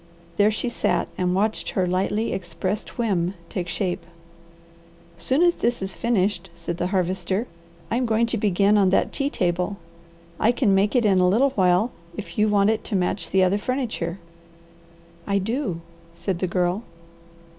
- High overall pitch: Yes, high, 195 Hz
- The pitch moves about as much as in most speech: Yes, average, 3.4 semitones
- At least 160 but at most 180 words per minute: Yes, average, 170 wpm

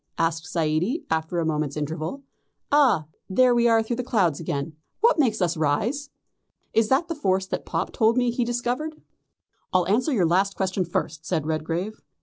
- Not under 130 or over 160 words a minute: No, average, 175 wpm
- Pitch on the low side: No, high, 190 Hz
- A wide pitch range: Yes, wide, 7.1 semitones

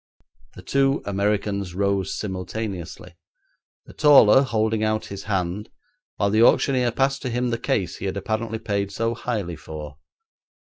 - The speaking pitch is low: Yes, low, 105 Hz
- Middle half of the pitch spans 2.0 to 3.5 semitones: Yes, average, 3.2 semitones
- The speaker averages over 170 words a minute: No, average, 145 wpm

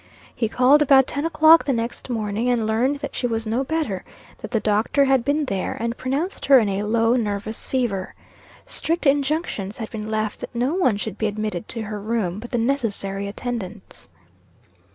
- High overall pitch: Yes, high, 230 Hz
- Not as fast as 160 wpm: No, average, 190 wpm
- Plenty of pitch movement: No, average, 4.2 semitones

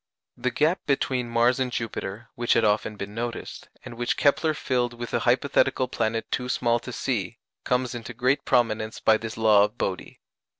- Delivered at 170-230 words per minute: Yes, average, 180 wpm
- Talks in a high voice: No, low, 120 Hz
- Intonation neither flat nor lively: No, narrow, 2.2 semitones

